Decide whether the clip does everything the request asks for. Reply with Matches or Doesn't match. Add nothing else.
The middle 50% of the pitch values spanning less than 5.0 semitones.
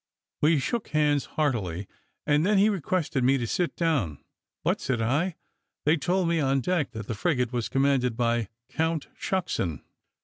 Doesn't match